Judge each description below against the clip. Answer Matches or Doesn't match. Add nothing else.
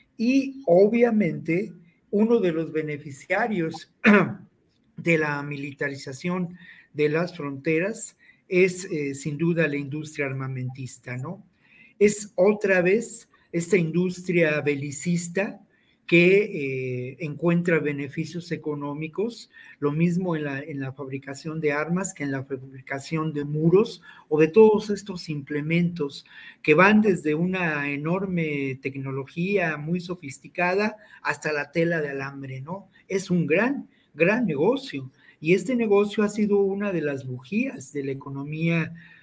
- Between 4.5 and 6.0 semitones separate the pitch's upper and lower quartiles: Matches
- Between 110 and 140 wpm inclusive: Matches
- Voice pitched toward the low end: Doesn't match